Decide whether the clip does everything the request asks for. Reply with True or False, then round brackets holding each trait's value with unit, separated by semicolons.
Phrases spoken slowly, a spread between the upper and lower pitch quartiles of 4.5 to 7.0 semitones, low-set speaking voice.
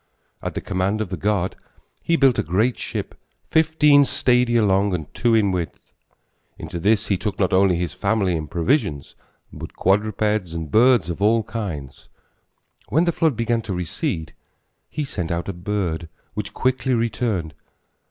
False (160 wpm; 4.8 semitones; 100 Hz)